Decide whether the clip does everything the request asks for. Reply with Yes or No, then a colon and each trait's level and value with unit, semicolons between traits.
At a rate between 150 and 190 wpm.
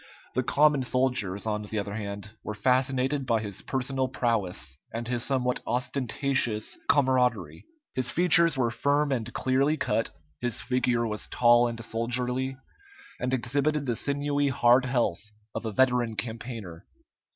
No: average, 140 wpm